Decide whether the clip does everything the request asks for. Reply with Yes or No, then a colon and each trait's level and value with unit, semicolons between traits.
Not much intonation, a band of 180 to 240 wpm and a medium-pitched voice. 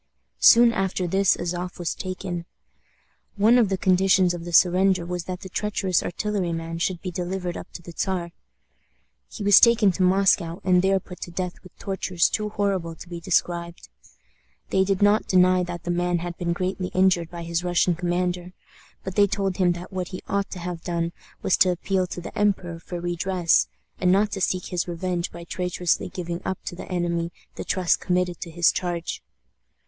Yes: narrow, 1.7 semitones; average, 190 wpm; medium, 180 Hz